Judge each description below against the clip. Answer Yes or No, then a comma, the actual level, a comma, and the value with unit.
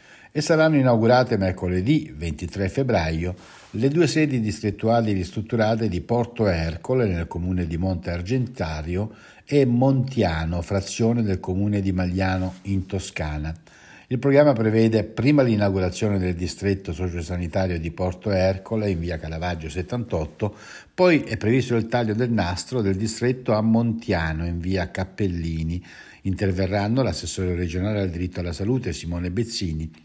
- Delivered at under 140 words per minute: Yes, average, 130 wpm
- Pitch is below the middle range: Yes, very low, 95 Hz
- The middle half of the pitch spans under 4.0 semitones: No, average, 4.4 semitones